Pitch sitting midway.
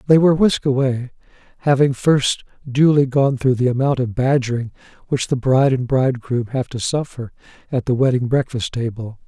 No: low, 130 Hz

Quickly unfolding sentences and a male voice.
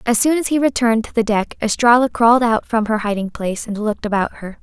No: fast, 245 wpm; female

